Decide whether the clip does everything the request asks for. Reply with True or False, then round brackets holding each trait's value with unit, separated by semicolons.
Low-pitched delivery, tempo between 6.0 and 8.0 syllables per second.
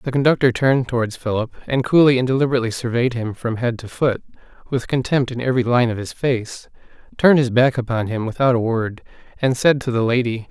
True (125 Hz; 6.2 syllables/s)